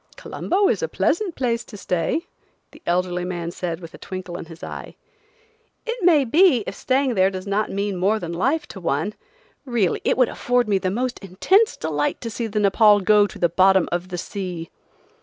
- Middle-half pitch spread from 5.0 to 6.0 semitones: Yes, wide, 5.6 semitones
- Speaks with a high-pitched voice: Yes, high, 200 Hz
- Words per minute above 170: Yes, average, 195 wpm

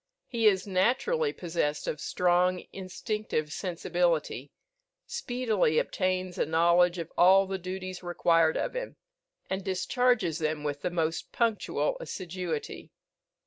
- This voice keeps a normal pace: No, slow, 120 wpm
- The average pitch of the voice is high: No, medium, 180 Hz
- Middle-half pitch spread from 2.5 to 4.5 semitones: Yes, average, 3.0 semitones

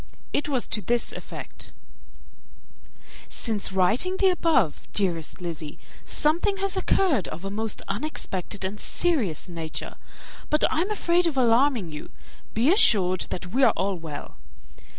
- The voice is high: Yes, high, 225 Hz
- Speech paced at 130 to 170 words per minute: Yes, average, 140 wpm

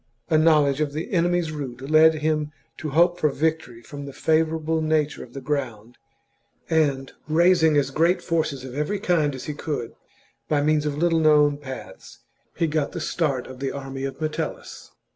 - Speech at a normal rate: Yes, average, 180 wpm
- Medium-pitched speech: Yes, medium, 150 Hz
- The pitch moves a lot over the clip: No, narrow, 2.4 semitones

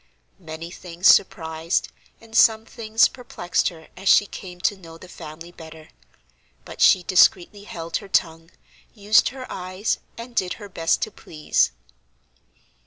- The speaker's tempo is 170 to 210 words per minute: No, average, 145 wpm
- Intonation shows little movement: No, average, 4.0 semitones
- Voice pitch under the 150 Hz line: No, medium, 180 Hz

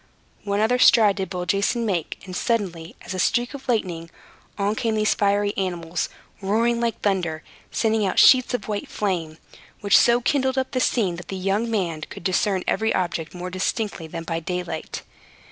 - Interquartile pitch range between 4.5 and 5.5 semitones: No, average, 4.0 semitones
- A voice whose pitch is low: No, high, 200 Hz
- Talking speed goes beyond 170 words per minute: Yes, average, 185 wpm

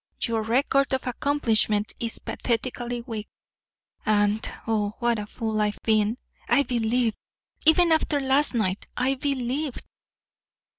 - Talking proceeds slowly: Yes, slow, 120 wpm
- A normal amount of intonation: Yes, average, 3.5 semitones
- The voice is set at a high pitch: Yes, high, 235 Hz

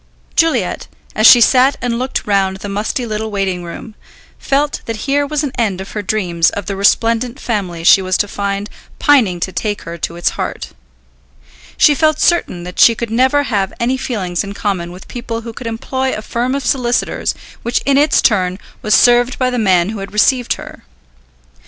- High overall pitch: Yes, high, 220 Hz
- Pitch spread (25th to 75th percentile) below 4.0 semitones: No, average, 4.6 semitones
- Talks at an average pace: Yes, average, 195 wpm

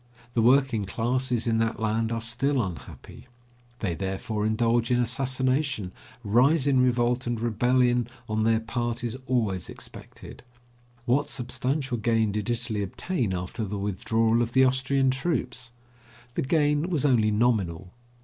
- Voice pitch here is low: Yes, low, 120 Hz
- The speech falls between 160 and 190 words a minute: No, average, 140 wpm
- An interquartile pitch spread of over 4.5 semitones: No, average, 2.9 semitones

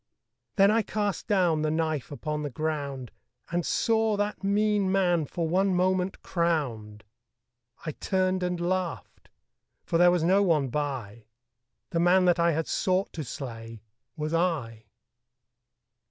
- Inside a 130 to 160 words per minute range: Yes, average, 140 wpm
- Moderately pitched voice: Yes, medium, 170 Hz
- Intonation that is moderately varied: Yes, average, 4.0 semitones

